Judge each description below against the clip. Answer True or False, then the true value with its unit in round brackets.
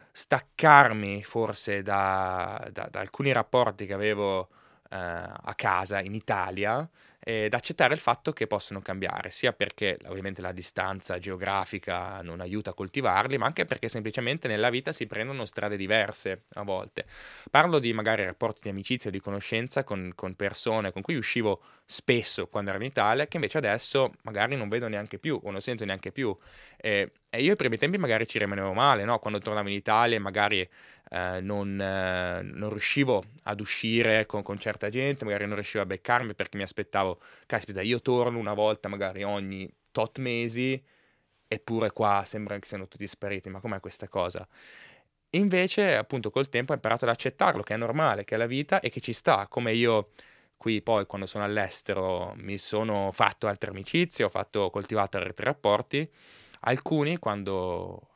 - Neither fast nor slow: False (175 wpm)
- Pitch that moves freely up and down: False (2.9 semitones)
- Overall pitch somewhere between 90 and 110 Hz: True (105 Hz)